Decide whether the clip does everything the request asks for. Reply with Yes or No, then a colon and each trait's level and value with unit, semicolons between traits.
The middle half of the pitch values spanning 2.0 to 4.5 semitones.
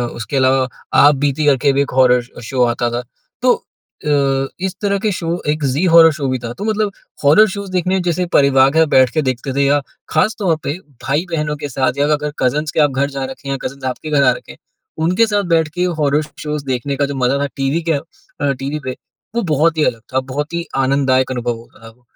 Yes: average, 3.5 semitones